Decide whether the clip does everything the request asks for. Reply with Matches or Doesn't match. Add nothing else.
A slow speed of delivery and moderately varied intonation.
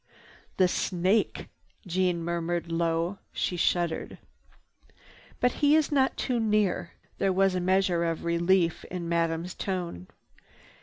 Doesn't match